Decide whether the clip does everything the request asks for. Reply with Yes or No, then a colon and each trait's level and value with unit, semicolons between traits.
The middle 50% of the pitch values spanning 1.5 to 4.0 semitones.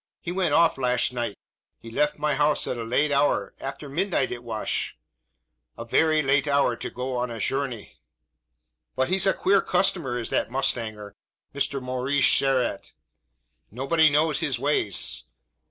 Yes: average, 3.6 semitones